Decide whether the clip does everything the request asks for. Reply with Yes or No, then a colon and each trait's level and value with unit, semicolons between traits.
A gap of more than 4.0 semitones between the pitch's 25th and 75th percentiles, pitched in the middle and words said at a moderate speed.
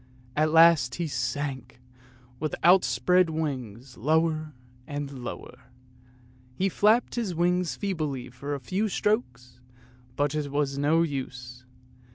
No: average, 4.7 semitones; medium, 145 Hz; slow, 120 wpm